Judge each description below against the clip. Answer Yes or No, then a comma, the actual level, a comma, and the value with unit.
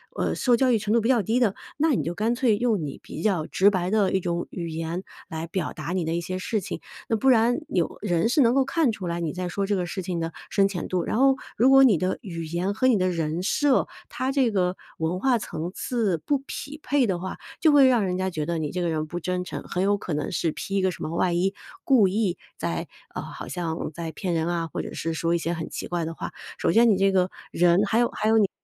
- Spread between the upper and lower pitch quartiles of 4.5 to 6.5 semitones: Yes, average, 4.9 semitones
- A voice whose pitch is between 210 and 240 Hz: No, medium, 185 Hz